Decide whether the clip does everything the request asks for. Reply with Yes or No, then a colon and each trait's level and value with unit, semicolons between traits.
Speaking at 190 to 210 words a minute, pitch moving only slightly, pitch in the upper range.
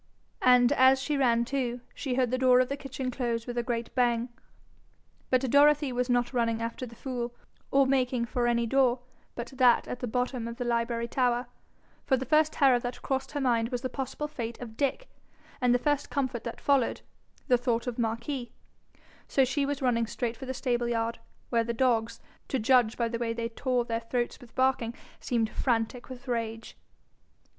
Yes: average, 195 wpm; narrow, 1.9 semitones; high, 245 Hz